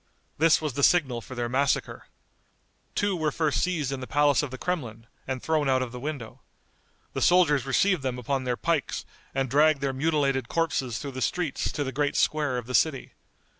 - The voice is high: No, medium, 140 Hz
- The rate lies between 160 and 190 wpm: No, average, 200 wpm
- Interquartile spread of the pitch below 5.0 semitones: Yes, average, 3.3 semitones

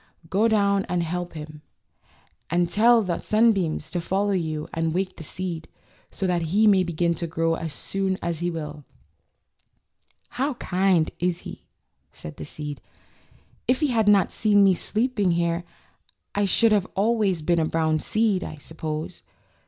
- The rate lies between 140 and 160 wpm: No, average, 175 wpm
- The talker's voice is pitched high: No, medium, 180 Hz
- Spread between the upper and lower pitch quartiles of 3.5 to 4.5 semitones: Yes, average, 3.8 semitones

